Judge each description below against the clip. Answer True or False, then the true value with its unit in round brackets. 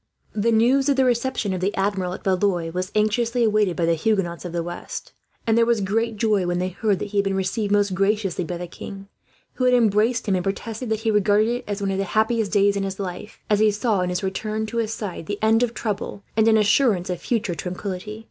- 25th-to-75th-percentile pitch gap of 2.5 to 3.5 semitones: True (2.9 semitones)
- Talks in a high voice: True (205 Hz)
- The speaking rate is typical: False (250 wpm)